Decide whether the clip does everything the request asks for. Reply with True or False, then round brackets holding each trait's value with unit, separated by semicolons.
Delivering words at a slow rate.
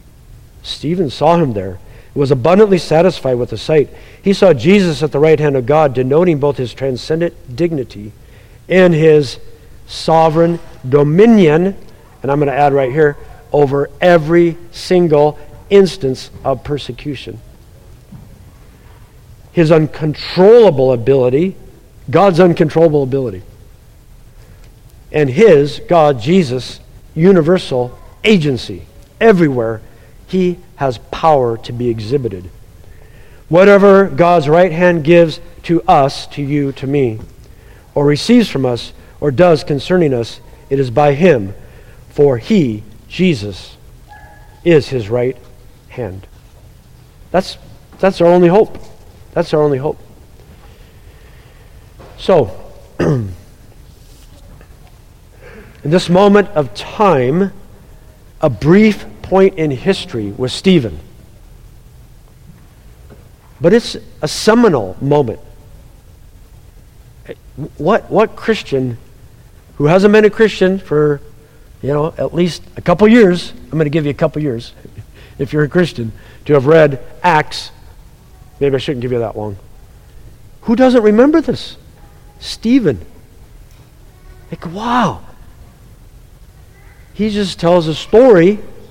True (115 wpm)